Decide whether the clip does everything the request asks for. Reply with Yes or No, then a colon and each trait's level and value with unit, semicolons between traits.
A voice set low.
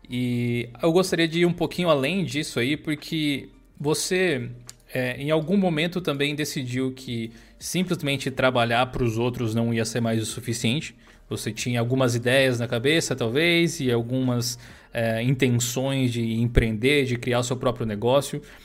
Yes: low, 130 Hz